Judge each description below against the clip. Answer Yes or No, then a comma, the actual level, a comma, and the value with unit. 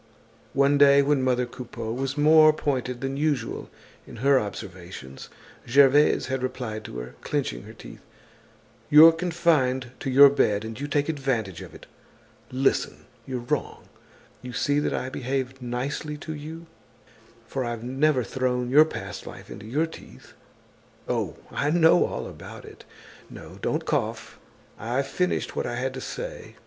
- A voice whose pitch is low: Yes, low, 130 Hz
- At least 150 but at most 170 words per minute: Yes, average, 155 wpm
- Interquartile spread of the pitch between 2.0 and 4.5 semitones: Yes, average, 3.2 semitones